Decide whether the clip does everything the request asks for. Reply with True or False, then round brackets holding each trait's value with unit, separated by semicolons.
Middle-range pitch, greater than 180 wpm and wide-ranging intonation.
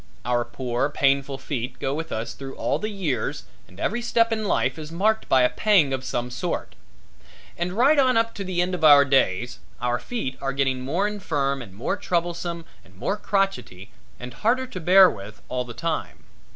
True (145 Hz; 195 wpm; 7.5 semitones)